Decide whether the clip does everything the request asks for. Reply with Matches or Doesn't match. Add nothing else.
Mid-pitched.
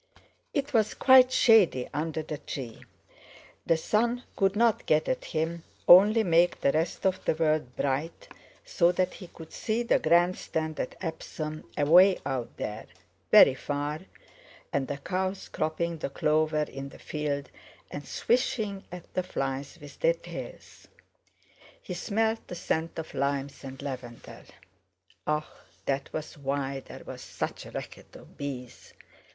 Matches